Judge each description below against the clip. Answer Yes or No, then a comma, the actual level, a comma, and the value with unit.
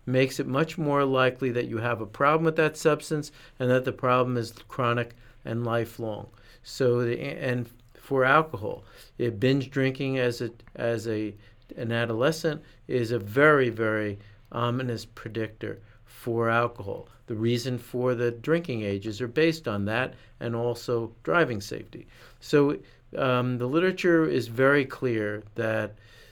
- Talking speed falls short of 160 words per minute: Yes, average, 150 wpm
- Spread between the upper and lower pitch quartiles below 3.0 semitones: Yes, narrow, 2.5 semitones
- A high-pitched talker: No, low, 120 Hz